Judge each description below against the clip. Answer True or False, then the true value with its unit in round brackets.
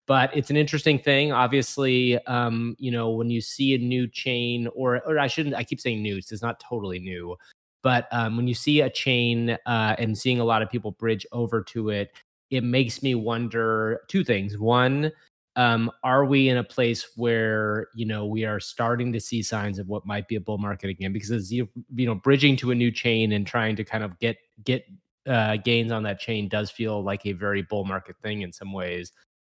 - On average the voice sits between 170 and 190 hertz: False (115 Hz)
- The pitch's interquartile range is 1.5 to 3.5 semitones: True (2.8 semitones)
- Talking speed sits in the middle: False (220 wpm)